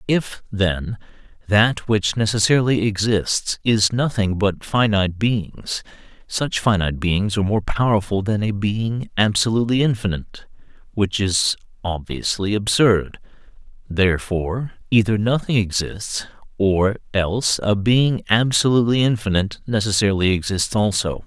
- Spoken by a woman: No, male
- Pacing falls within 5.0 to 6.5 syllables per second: No, 4.6 syllables/s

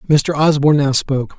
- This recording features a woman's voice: No, male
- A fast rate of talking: No, average, 175 wpm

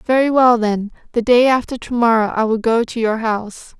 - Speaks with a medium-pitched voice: No, high, 230 Hz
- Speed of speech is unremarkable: No, fast, 220 wpm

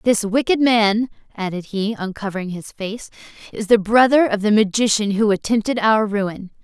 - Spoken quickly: No, average, 165 wpm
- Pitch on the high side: Yes, high, 215 Hz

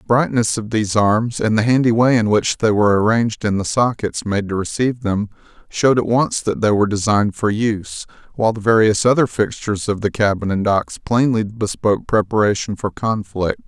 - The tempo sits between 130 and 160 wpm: No, average, 195 wpm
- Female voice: No, male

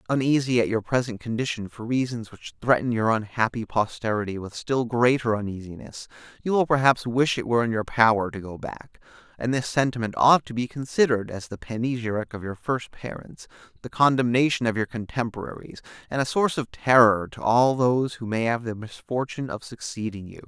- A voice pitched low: Yes, low, 120 Hz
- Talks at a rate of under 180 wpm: No, average, 185 wpm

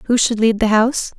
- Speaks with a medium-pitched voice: No, high, 225 Hz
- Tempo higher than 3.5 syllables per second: Yes, 5.4 syllables/s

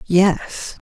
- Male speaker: No, female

